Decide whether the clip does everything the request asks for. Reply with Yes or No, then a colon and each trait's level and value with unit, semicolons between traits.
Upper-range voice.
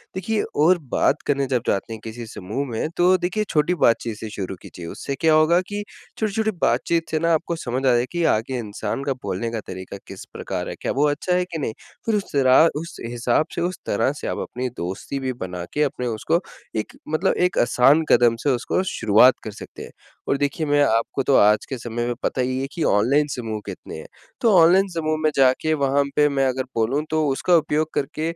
No: low, 135 Hz